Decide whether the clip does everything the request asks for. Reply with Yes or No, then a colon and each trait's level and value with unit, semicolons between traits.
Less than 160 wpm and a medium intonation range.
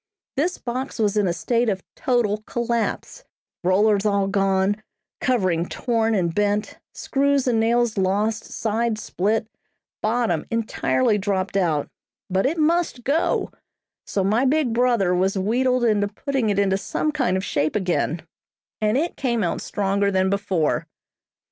Yes: average, 145 wpm; average, 3.8 semitones